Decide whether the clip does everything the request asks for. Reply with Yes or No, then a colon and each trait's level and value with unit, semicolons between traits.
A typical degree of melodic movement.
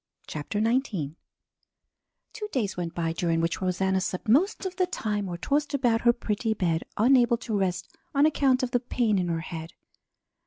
No: wide, 6.4 semitones